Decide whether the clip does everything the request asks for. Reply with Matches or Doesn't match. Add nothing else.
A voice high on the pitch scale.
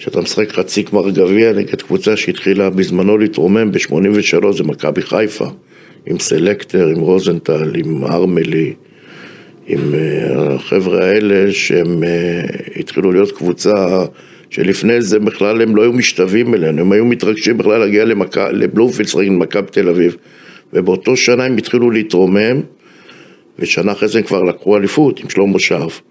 Doesn't match